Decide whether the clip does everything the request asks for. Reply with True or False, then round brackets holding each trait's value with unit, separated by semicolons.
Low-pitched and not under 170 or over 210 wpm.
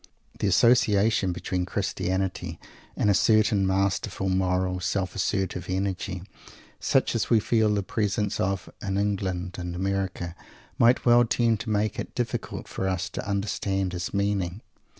False (95 Hz; 145 wpm)